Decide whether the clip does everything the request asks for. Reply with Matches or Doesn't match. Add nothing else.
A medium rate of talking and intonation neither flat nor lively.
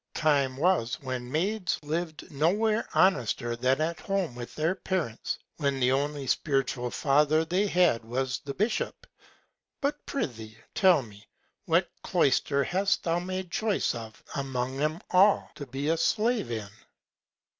Doesn't match